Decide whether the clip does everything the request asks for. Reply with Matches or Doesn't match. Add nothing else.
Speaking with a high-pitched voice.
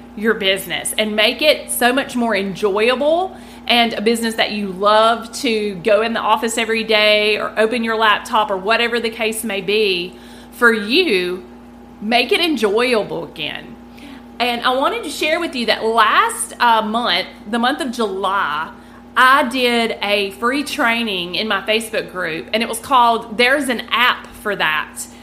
Matches